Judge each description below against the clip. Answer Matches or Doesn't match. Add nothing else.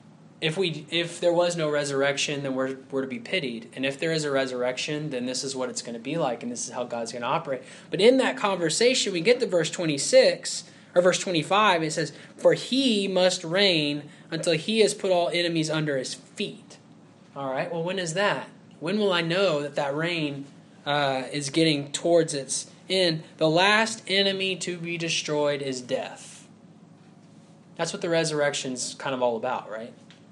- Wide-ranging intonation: Doesn't match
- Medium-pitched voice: Matches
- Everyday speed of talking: Matches